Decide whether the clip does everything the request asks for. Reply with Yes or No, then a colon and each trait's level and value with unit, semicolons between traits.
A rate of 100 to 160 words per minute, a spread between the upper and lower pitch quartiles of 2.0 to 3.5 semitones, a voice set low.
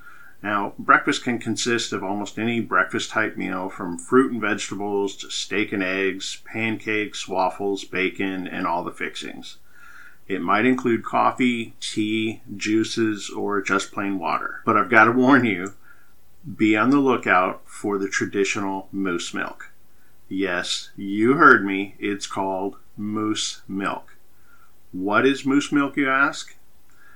Yes: average, 140 wpm; average, 2.8 semitones; low, 105 Hz